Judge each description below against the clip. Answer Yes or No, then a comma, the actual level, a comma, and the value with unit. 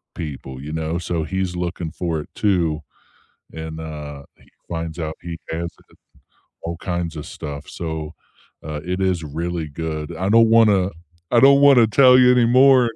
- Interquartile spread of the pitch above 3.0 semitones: Yes, average, 4.1 semitones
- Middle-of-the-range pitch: No, very low, 85 Hz